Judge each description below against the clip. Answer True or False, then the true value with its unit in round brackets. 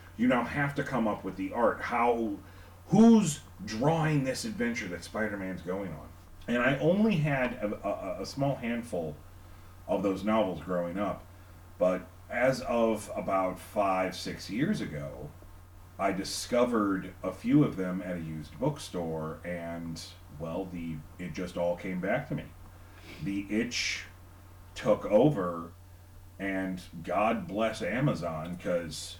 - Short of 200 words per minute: True (140 wpm)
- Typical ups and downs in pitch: True (3.8 semitones)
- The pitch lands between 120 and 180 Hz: False (90 Hz)